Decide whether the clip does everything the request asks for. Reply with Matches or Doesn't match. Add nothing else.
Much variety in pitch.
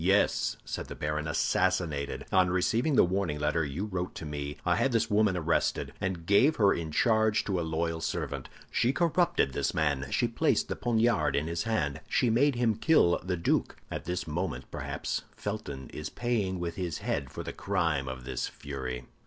Matches